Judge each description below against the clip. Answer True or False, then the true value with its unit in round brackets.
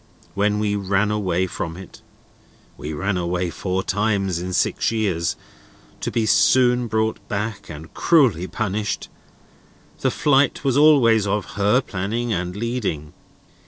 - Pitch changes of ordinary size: True (3.7 semitones)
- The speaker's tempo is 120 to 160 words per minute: True (135 wpm)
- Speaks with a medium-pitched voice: False (105 Hz)